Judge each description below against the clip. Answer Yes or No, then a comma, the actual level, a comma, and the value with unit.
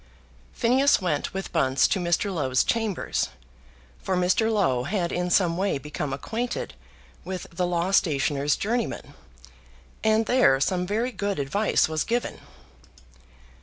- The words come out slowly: Yes, slow, 130 wpm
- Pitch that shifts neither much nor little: No, wide, 6.1 semitones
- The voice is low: No, medium, 180 Hz